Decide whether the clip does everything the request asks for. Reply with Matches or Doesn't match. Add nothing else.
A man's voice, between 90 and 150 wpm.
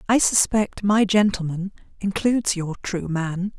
Doesn't match